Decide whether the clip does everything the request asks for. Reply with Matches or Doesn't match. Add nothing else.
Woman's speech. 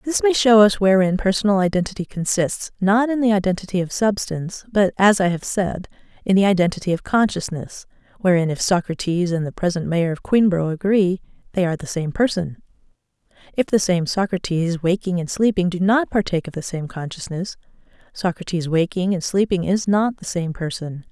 Matches